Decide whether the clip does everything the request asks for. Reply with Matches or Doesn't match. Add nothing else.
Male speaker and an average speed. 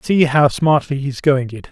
Doesn't match